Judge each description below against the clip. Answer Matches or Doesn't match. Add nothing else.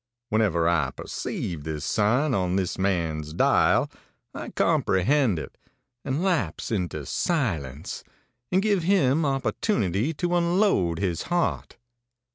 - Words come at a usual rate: Doesn't match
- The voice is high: Doesn't match